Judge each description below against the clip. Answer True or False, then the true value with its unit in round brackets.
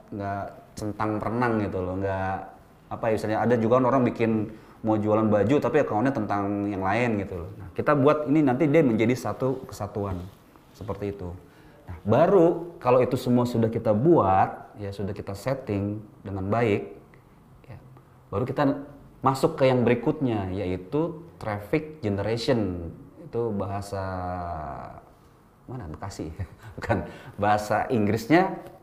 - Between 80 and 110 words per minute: False (135 wpm)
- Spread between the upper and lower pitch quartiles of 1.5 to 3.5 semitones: False (4.3 semitones)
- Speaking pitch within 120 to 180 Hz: False (110 Hz)